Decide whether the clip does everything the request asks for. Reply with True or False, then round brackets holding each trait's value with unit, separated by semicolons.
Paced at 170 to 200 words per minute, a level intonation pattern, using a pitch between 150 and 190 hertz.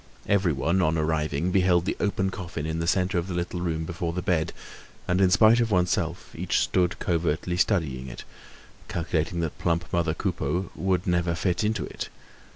False (175 wpm; 2.1 semitones; 85 Hz)